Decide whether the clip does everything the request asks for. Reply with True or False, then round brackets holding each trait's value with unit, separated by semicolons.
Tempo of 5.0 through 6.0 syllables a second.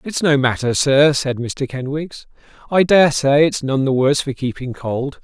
False (4.5 syllables/s)